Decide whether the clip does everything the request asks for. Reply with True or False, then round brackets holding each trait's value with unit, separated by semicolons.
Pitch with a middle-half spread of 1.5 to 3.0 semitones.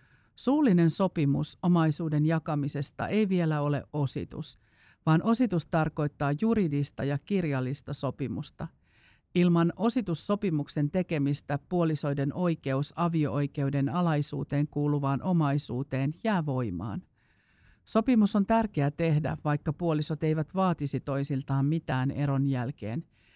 False (3.4 semitones)